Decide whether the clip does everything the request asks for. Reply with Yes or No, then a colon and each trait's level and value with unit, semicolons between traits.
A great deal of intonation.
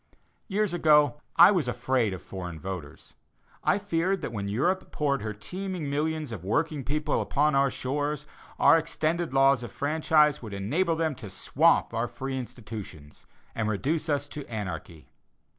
Yes: wide, 6.4 semitones